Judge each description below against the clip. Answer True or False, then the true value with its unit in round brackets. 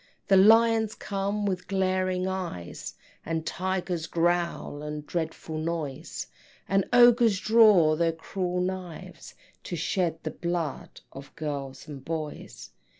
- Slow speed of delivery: True (120 wpm)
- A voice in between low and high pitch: True (175 Hz)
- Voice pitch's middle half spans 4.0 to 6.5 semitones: False (3.2 semitones)